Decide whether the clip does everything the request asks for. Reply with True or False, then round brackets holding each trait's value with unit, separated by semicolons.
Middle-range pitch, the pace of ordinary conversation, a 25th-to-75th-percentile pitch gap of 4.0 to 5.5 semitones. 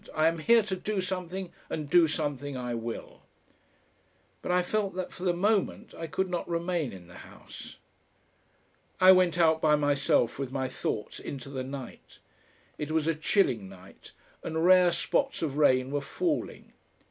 True (160 Hz; 170 wpm; 4.8 semitones)